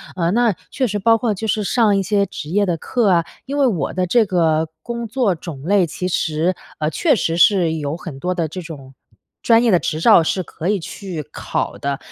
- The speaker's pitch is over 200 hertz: No, medium, 185 Hz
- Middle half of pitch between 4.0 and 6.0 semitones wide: Yes, average, 4.8 semitones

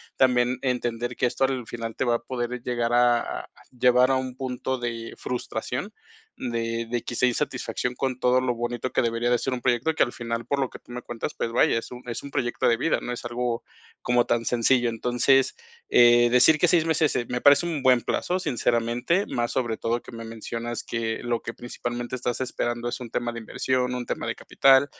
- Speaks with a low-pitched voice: Yes, low, 120 Hz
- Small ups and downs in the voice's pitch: Yes, narrow, 1.4 semitones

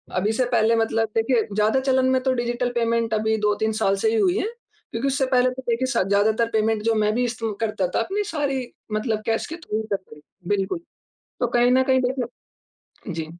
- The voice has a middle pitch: No, high, 230 Hz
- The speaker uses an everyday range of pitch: Yes, average, 3.1 semitones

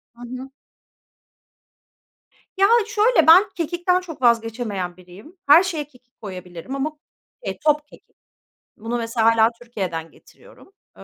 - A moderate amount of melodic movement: No, wide, 6.7 semitones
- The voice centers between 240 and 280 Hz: Yes, very high, 250 Hz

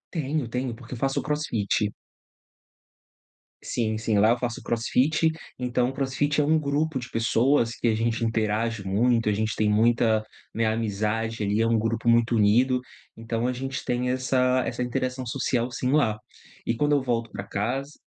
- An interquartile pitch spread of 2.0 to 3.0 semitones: Yes, narrow, 2.6 semitones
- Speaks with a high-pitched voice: No, low, 120 Hz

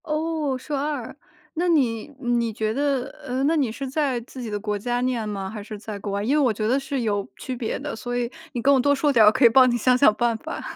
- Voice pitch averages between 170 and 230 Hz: No, high, 245 Hz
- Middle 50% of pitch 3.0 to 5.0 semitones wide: Yes, average, 3.9 semitones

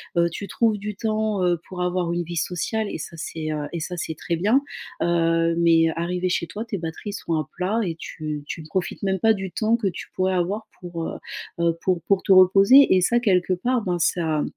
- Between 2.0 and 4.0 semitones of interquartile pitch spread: Yes, average, 3.3 semitones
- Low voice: No, medium, 180 Hz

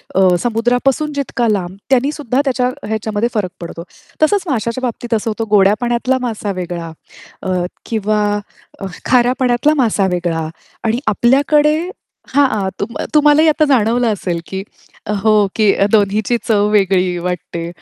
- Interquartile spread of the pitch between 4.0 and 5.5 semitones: Yes, average, 4.5 semitones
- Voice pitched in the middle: No, high, 225 Hz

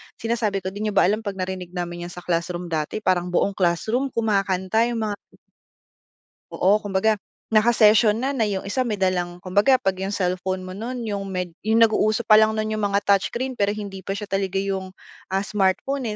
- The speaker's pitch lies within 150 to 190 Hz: No, high, 200 Hz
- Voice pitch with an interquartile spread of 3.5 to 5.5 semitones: No, average, 2.7 semitones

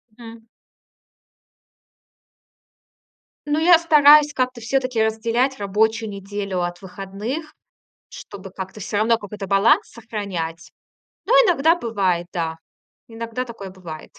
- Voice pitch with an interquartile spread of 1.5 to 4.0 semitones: No, average, 4.6 semitones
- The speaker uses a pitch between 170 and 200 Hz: No, high, 220 Hz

